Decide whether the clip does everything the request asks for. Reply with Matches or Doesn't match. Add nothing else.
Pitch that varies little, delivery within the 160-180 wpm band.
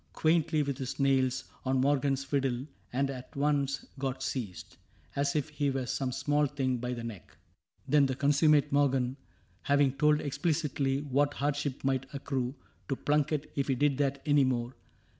Matches